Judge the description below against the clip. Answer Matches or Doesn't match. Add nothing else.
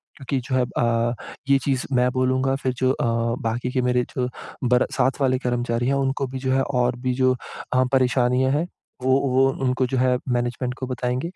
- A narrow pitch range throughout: Matches